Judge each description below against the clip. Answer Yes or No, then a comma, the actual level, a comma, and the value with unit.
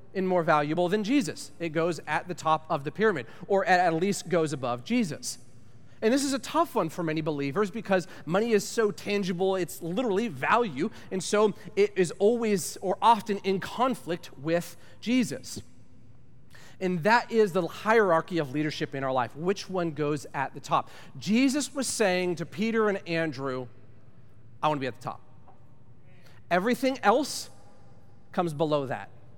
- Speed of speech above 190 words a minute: No, average, 165 wpm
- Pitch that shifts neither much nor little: No, wide, 7.4 semitones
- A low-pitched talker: No, medium, 170 Hz